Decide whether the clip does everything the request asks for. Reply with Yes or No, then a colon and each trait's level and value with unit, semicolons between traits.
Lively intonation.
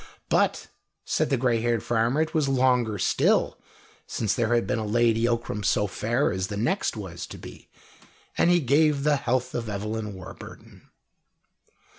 No: average, 3.4 semitones